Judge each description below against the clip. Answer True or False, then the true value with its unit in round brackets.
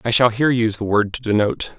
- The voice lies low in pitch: True (115 Hz)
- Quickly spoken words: True (270 wpm)